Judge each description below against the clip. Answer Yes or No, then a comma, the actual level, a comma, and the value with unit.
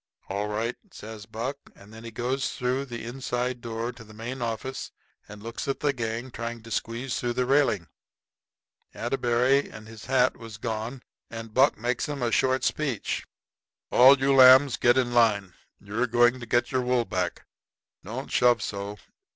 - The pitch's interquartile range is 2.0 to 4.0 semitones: Yes, narrow, 2.5 semitones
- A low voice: Yes, low, 120 Hz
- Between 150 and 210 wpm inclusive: Yes, average, 175 wpm